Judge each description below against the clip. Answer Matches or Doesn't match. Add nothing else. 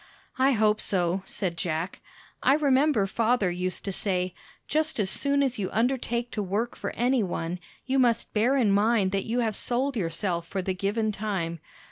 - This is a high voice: Matches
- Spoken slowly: Doesn't match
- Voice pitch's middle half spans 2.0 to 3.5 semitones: Doesn't match